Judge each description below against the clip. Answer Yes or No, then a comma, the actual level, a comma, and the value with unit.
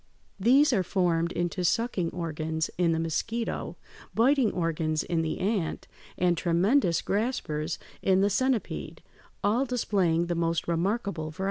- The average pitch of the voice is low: No, medium, 175 Hz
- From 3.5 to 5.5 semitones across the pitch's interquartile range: Yes, average, 4.8 semitones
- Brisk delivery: No, slow, 135 wpm